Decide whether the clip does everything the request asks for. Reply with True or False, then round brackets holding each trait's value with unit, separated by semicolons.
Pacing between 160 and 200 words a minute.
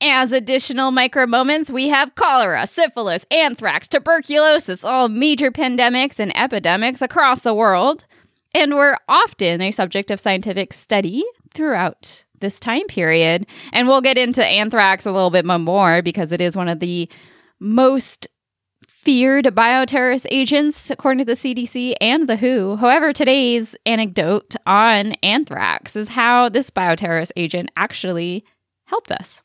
False (140 wpm)